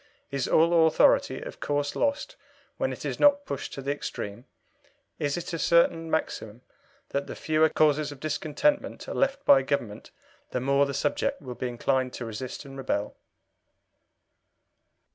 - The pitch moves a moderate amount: Yes, average, 3.6 semitones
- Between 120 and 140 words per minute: No, average, 160 wpm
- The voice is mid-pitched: Yes, medium, 145 Hz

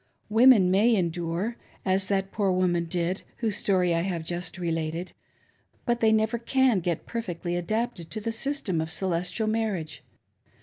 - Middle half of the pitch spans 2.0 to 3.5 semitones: No, average, 4.2 semitones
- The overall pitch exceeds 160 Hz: Yes, high, 190 Hz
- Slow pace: No, average, 150 wpm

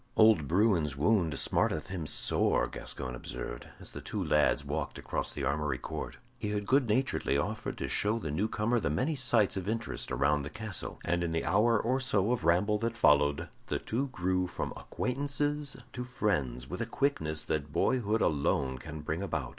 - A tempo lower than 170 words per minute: No, average, 185 wpm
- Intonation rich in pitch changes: Yes, wide, 7.4 semitones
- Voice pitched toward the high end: No, very low, 95 Hz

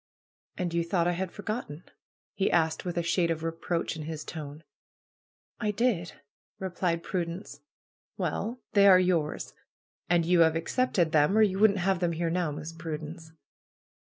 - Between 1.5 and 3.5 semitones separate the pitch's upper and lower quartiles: Yes, narrow, 2.6 semitones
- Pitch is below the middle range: No, medium, 170 Hz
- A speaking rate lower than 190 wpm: Yes, average, 165 wpm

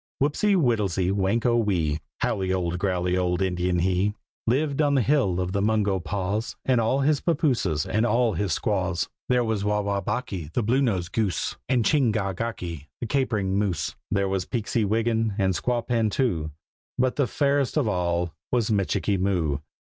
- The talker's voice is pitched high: No, low, 105 Hz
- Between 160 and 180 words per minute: Yes, average, 170 wpm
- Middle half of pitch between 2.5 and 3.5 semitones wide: No, average, 4.7 semitones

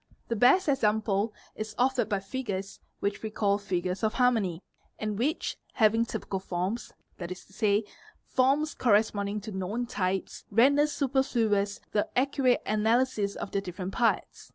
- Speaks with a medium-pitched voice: No, high, 215 Hz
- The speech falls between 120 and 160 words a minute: Yes, average, 155 wpm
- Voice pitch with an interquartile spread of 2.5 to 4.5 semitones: Yes, average, 3.7 semitones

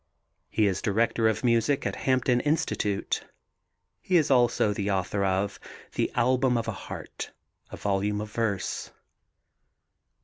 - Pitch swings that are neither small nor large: Yes, average, 3.6 semitones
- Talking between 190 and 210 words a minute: No, slow, 135 wpm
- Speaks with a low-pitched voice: Yes, low, 110 Hz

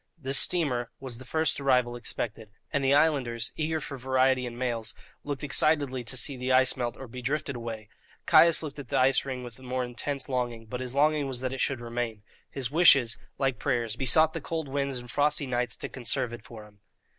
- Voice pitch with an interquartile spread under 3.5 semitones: Yes, average, 2.7 semitones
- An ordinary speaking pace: No, fast, 210 wpm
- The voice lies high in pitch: No, low, 130 Hz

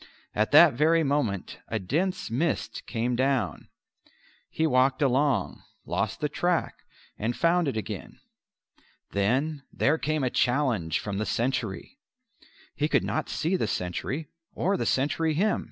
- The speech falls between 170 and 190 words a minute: No, average, 140 wpm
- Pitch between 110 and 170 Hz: Yes, medium, 140 Hz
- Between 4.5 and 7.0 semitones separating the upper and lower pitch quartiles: Yes, wide, 5.4 semitones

